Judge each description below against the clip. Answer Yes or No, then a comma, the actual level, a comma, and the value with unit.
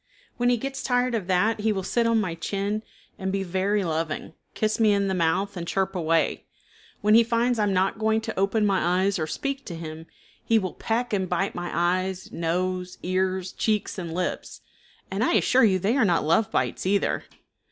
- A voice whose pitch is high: Yes, high, 195 Hz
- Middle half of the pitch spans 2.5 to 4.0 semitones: Yes, average, 3.5 semitones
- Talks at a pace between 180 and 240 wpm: Yes, fast, 205 wpm